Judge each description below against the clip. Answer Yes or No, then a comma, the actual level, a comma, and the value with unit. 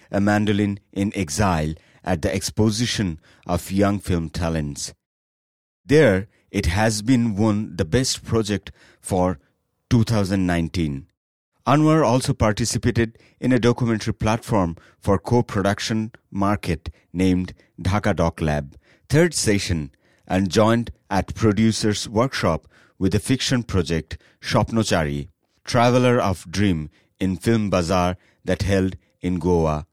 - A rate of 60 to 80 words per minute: No, average, 115 wpm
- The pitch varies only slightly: No, average, 4.1 semitones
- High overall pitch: No, low, 100 Hz